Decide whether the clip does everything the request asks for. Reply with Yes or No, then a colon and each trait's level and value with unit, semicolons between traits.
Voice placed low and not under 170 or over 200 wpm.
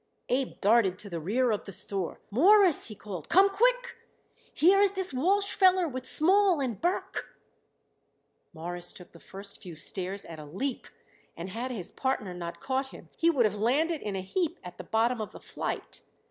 No: high, 240 Hz; average, 190 wpm